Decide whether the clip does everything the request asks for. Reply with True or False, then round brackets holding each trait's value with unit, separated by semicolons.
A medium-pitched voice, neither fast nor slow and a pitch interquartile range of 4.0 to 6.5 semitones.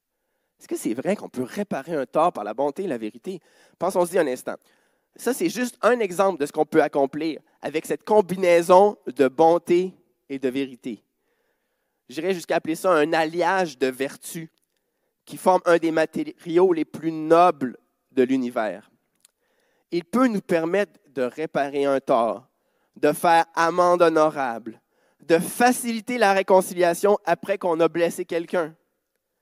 True (170 Hz; 155 wpm; 4.6 semitones)